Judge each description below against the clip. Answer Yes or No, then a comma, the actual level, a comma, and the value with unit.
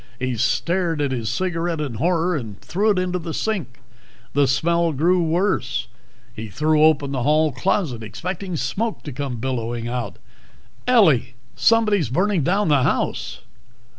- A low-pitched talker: No, medium, 155 Hz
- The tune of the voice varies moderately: No, wide, 6.2 semitones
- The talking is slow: No, average, 150 wpm